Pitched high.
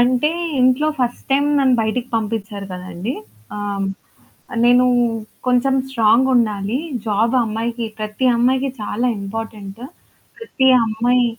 Yes: high, 235 Hz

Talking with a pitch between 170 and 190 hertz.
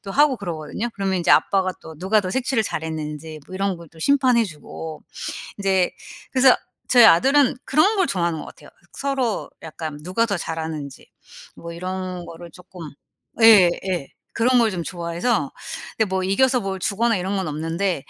Yes: medium, 185 Hz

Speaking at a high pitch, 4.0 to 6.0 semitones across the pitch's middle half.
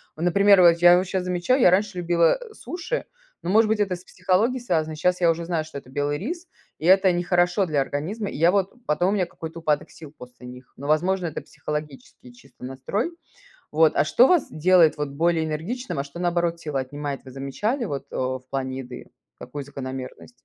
No: medium, 170 Hz; average, 4.5 semitones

